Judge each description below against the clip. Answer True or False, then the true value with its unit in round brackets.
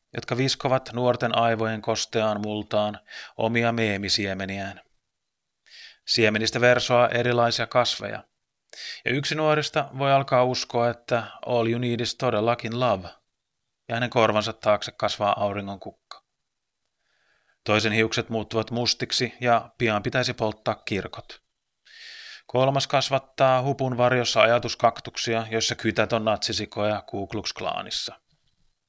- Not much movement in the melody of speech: True (2.3 semitones)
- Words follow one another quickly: False (105 wpm)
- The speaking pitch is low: True (115 Hz)